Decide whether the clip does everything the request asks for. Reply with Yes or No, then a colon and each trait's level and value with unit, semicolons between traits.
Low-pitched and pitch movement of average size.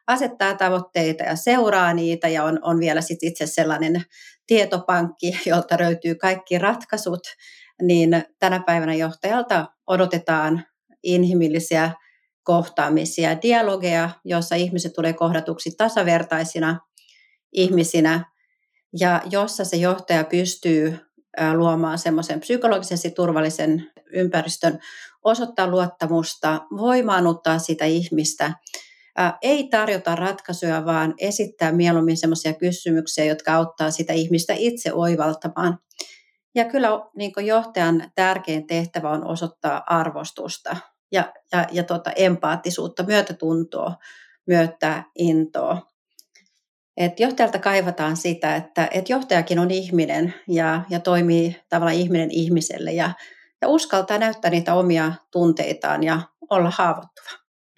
No: medium, 175 Hz; average, 3.0 semitones